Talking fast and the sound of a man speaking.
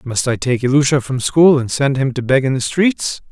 Yes: fast, 255 wpm; male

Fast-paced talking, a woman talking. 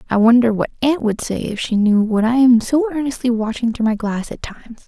Yes: fast, 245 wpm; female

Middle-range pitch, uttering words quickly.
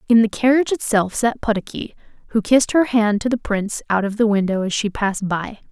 No: high, 220 Hz; fast, 220 wpm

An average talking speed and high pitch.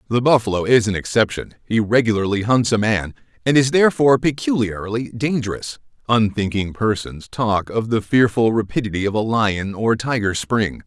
No: average, 155 wpm; low, 110 Hz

